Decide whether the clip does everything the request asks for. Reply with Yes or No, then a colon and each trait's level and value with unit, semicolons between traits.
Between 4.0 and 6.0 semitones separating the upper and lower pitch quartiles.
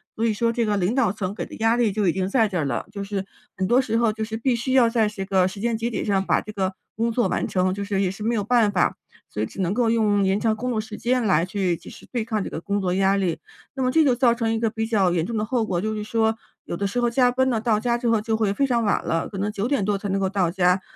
No: average, 3.2 semitones